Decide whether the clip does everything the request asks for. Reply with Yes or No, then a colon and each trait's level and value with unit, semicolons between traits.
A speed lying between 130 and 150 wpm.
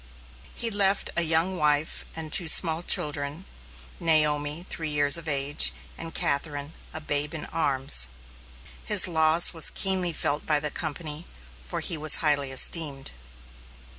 Yes: average, 140 wpm